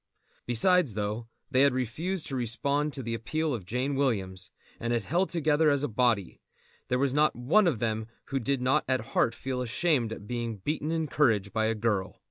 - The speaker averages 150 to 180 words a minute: No, average, 200 wpm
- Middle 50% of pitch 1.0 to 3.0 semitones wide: No, average, 4.6 semitones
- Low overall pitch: Yes, low, 125 Hz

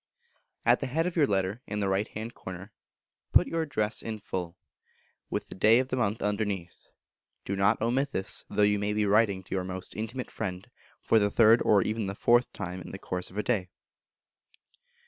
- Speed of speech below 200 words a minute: No, fast, 205 wpm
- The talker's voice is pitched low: Yes, low, 105 Hz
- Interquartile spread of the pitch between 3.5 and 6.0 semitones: No, average, 3.1 semitones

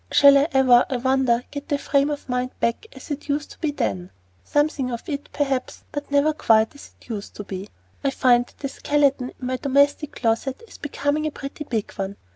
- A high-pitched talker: Yes, very high, 275 Hz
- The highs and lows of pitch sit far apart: No, average, 3.0 semitones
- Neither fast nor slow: No, fast, 215 wpm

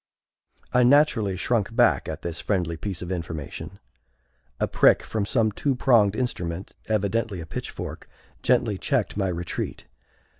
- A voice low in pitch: Yes, low, 100 Hz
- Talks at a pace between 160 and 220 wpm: No, average, 140 wpm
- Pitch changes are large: No, average, 4.7 semitones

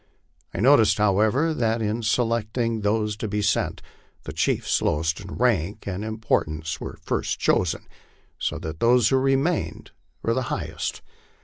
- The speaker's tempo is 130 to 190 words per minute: Yes, average, 145 wpm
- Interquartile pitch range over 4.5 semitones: No, average, 2.8 semitones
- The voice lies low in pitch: Yes, low, 110 Hz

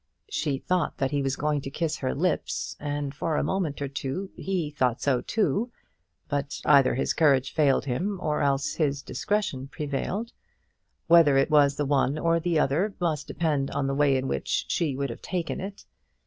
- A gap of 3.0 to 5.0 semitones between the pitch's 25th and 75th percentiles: Yes, average, 3.5 semitones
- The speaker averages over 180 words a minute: Yes, average, 190 wpm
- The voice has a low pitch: No, medium, 145 Hz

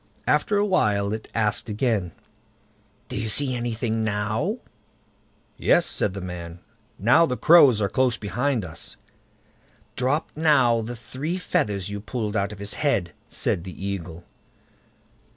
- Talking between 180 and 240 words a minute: No, average, 140 wpm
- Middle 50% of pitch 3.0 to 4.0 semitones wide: No, average, 4.4 semitones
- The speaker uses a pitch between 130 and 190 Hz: No, low, 110 Hz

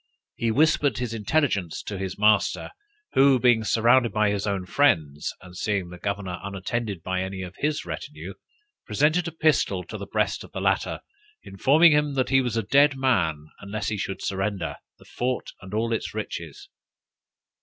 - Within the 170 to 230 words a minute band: Yes, average, 175 wpm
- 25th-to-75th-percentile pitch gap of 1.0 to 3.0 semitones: No, wide, 5.6 semitones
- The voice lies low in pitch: Yes, low, 110 Hz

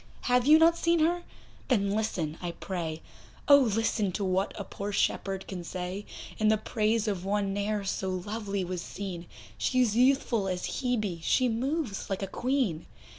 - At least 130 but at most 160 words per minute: No, average, 170 wpm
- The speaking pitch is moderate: No, high, 205 Hz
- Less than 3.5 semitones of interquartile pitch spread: No, average, 4.6 semitones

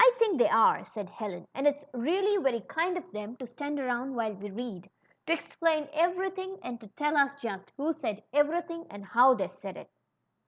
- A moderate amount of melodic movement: No, wide, 6.5 semitones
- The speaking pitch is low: No, very high, 275 Hz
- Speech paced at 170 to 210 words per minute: Yes, average, 200 wpm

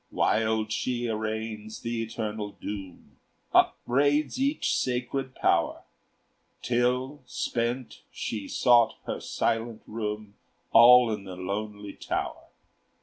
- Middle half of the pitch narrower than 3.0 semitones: Yes, narrow, 2.6 semitones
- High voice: No, low, 115 Hz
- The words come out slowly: Yes, slow, 100 wpm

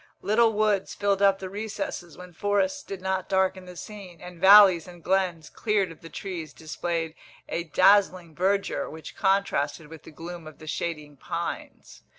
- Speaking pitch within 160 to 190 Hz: Yes, medium, 185 Hz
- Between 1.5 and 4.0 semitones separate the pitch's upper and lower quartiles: Yes, average, 3.2 semitones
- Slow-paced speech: No, average, 165 wpm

